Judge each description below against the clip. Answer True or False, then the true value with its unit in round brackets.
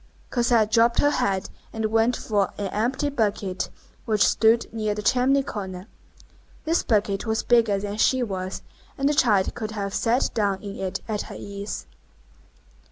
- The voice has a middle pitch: False (215 Hz)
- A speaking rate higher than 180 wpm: False (165 wpm)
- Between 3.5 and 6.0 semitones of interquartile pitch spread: False (3.0 semitones)